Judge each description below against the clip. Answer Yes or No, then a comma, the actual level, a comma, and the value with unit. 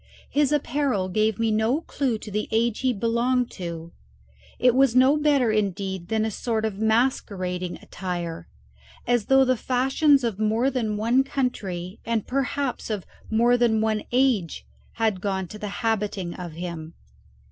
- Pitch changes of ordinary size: Yes, average, 4.5 semitones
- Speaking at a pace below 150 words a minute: No, average, 160 wpm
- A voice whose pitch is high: Yes, high, 220 Hz